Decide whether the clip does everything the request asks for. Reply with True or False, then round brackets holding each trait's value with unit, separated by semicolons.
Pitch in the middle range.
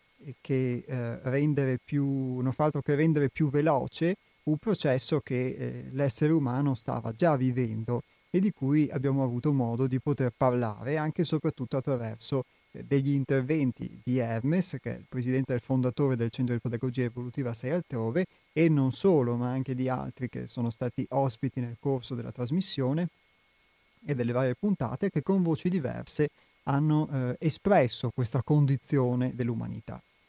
False (130 Hz)